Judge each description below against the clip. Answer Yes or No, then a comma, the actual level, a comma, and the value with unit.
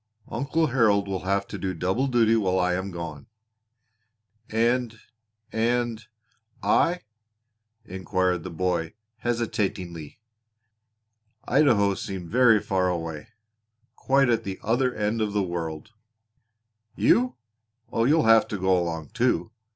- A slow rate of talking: Yes, slow, 120 wpm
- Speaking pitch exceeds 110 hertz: No, low, 105 Hz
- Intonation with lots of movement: No, average, 4.5 semitones